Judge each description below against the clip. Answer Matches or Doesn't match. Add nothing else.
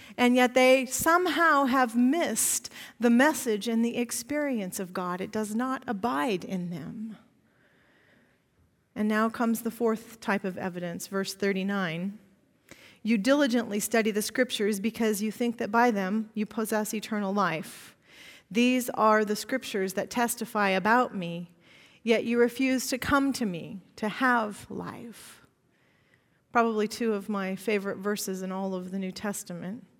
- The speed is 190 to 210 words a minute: Doesn't match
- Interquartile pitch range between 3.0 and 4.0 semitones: Matches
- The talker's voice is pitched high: Matches